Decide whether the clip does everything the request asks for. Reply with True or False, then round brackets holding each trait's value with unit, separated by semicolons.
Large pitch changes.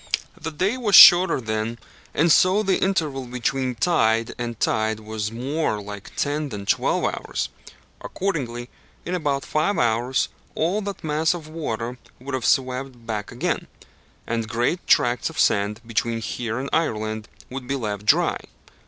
True (5.8 semitones)